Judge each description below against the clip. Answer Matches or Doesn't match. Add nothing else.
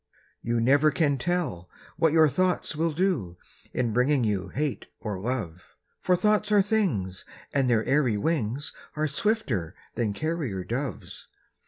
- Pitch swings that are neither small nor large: Doesn't match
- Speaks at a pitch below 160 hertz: Matches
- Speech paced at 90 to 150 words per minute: Matches